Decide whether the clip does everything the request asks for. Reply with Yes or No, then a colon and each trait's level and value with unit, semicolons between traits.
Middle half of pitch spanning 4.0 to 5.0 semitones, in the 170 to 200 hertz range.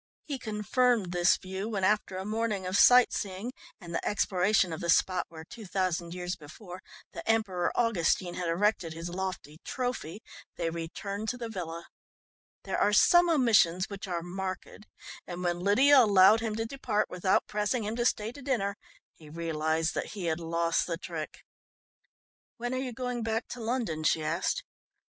Yes: average, 4.6 semitones; high, 190 Hz